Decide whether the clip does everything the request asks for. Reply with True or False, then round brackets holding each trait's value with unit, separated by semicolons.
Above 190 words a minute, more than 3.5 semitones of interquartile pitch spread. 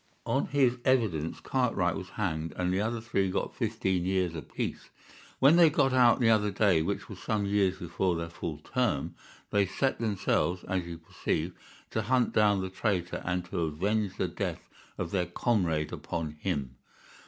False (175 wpm; 4.4 semitones)